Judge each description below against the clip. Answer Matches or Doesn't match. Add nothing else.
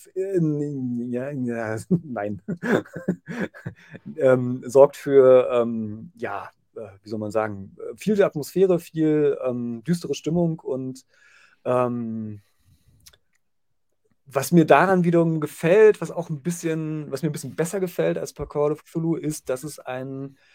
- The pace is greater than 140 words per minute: Doesn't match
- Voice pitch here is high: Doesn't match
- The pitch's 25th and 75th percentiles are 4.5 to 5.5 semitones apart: Matches